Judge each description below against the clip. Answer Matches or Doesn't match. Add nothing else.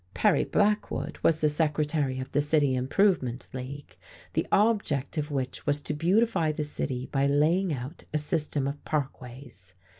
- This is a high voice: Doesn't match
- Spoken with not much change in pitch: Doesn't match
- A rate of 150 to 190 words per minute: Matches